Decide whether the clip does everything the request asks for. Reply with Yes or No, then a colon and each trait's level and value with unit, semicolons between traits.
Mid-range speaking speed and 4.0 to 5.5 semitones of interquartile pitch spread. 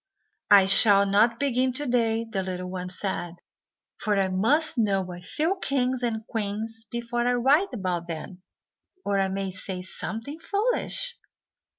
Yes: average, 155 wpm; average, 4.7 semitones